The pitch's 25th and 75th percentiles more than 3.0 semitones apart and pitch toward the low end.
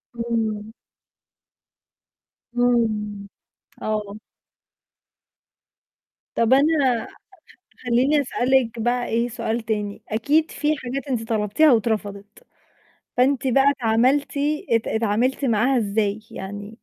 No: average, 3.5 semitones; high, 230 Hz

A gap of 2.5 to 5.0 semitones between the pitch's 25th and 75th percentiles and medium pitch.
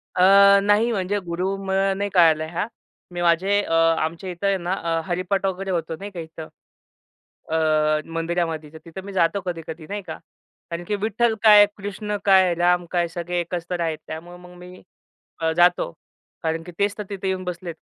Yes: average, 2.8 semitones; medium, 180 Hz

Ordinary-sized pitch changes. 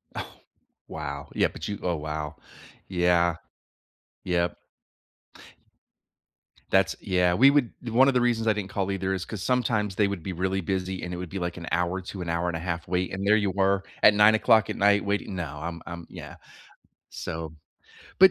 Yes: average, 3.0 semitones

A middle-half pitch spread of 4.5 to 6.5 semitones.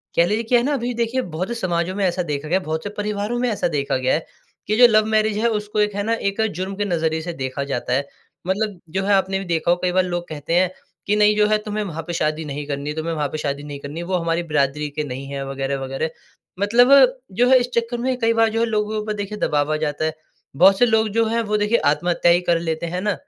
Yes: wide, 5.5 semitones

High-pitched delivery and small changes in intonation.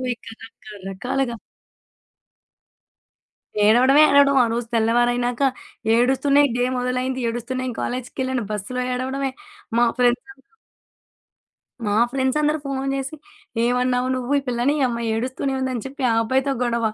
Yes: very high, 255 Hz; narrow, 1.9 semitones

